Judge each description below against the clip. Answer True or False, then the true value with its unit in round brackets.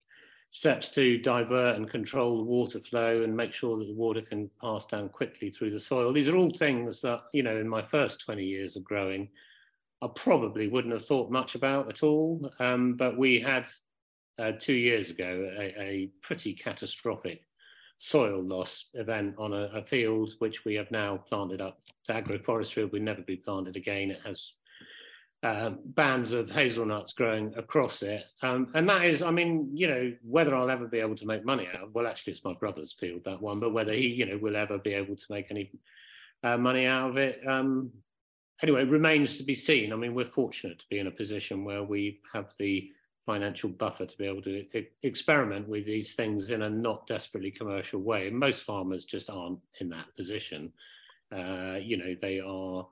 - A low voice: True (110 Hz)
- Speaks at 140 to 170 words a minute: False (200 wpm)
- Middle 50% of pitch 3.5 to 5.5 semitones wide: True (4.0 semitones)